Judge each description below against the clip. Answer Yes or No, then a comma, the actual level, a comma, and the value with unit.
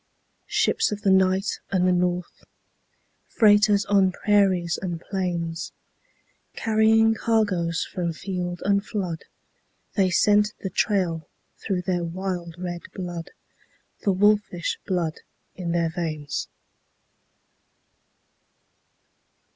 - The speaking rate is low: Yes, slow, 100 wpm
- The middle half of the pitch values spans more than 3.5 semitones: No, average, 2.8 semitones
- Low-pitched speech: No, medium, 185 Hz